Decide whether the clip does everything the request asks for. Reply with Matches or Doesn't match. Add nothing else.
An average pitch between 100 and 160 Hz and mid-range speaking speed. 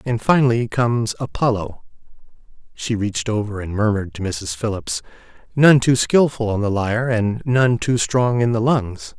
Matches